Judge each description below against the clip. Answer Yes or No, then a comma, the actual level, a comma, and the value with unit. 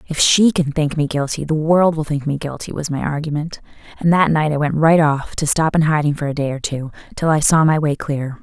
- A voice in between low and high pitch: Yes, medium, 150 Hz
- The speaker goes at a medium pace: No, fast, 265 wpm